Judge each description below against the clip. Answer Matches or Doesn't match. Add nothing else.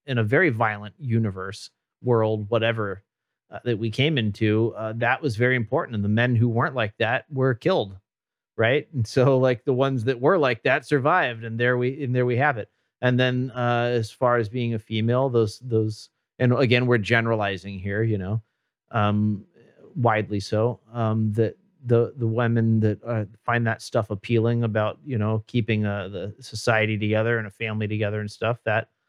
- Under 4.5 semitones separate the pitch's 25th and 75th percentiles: Matches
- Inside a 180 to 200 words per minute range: Matches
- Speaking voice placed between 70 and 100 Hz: Doesn't match